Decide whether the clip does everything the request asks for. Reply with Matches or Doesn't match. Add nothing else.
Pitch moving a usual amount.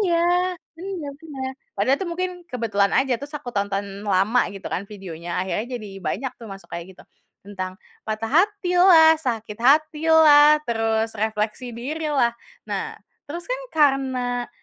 Doesn't match